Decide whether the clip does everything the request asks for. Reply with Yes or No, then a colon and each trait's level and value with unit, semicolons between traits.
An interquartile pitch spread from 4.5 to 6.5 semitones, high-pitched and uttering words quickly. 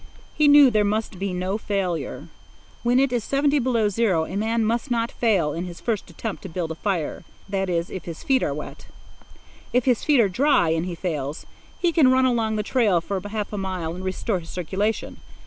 Yes: average, 4.9 semitones; high, 205 Hz; fast, 215 wpm